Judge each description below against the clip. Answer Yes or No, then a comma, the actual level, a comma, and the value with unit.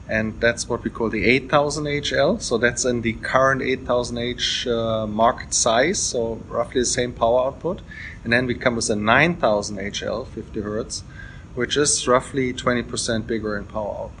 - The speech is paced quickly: No, average, 175 wpm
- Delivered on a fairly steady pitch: Yes, narrow, 2.2 semitones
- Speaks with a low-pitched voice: Yes, low, 120 Hz